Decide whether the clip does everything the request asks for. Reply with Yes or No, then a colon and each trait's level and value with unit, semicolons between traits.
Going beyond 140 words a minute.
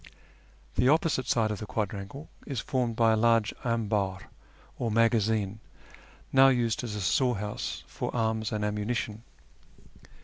No: slow, 135 wpm